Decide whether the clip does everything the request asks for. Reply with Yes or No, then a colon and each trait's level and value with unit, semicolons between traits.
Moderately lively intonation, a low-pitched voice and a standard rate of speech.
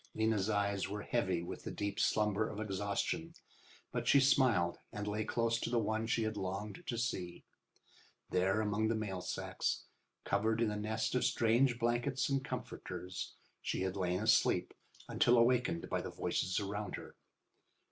Yes: average, 3.0 semitones; low, 110 Hz; average, 165 wpm